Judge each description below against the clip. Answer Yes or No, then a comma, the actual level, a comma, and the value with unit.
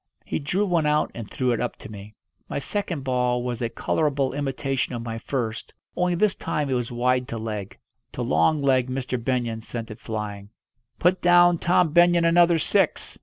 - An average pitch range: No, wide, 5.8 semitones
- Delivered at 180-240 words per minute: Yes, average, 190 wpm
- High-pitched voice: No, low, 130 Hz